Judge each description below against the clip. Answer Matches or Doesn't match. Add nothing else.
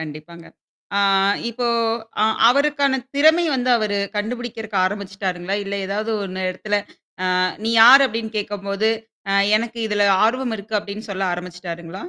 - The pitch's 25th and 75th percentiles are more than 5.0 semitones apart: Doesn't match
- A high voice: Matches